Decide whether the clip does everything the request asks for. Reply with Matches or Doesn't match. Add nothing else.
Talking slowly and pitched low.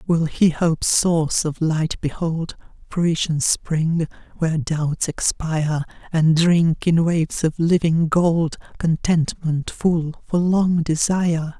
Doesn't match